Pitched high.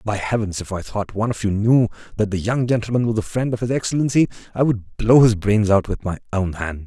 No: low, 110 Hz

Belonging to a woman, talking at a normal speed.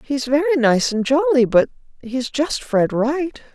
Yes: female; average, 170 wpm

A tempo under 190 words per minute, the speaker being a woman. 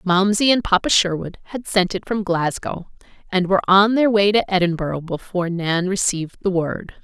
Yes: average, 180 wpm; female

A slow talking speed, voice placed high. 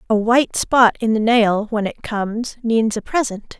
No: average, 200 wpm; high, 225 Hz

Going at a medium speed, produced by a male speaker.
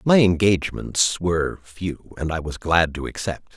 Yes: average, 170 wpm; male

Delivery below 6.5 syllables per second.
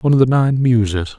Yes: 6.1 syllables/s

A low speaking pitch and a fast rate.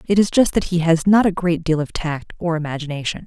No: medium, 165 Hz; fast, 255 wpm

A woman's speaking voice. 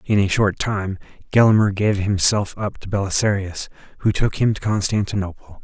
No: male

